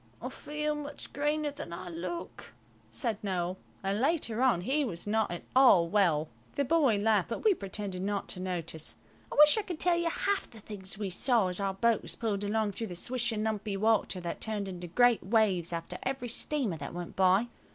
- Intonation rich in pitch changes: Yes, wide, 5.7 semitones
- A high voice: Yes, high, 210 Hz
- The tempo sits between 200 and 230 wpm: Yes, fast, 205 wpm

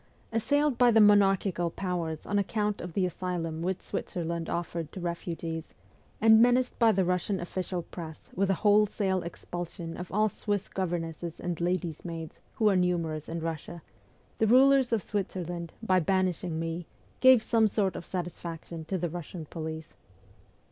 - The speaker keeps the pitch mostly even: No, average, 3.6 semitones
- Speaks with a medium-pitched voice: Yes, medium, 180 Hz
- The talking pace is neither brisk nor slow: Yes, average, 155 wpm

